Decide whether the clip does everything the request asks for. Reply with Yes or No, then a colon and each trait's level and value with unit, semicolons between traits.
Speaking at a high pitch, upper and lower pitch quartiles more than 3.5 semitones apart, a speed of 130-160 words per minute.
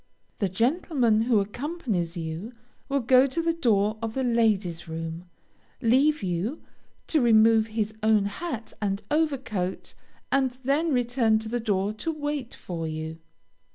Yes: high, 225 Hz; average, 5.2 semitones; average, 150 wpm